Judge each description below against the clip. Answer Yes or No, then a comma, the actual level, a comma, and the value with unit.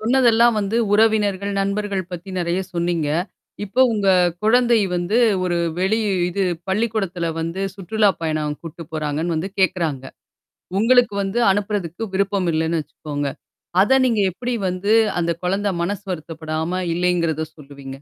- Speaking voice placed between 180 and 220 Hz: Yes, medium, 185 Hz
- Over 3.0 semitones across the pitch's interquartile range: Yes, average, 4.0 semitones